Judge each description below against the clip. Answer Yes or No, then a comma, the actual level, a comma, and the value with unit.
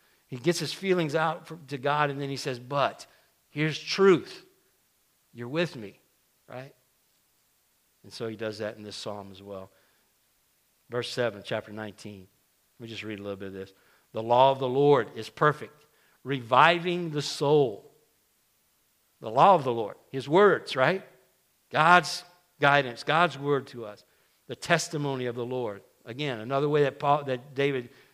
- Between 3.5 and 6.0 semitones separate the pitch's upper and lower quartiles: Yes, average, 5.3 semitones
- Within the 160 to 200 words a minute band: Yes, average, 165 wpm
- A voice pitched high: No, low, 135 Hz